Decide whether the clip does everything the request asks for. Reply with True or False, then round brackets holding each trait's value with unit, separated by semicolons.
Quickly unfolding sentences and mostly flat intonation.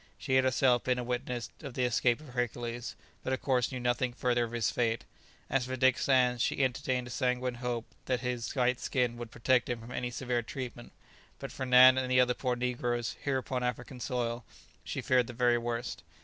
True (210 wpm; 1.0 semitones)